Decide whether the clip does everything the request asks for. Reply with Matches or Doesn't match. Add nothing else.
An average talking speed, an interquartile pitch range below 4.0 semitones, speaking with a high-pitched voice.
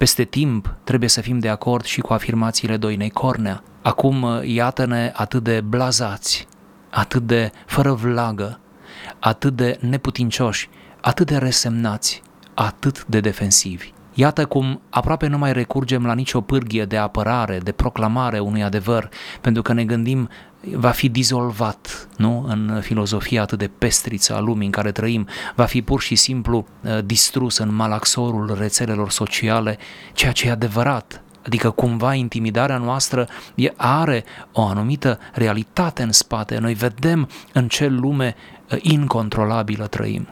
Doesn't match